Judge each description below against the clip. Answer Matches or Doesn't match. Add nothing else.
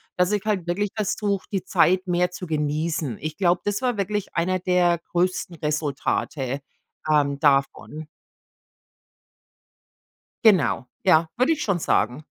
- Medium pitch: Matches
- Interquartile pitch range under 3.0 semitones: Doesn't match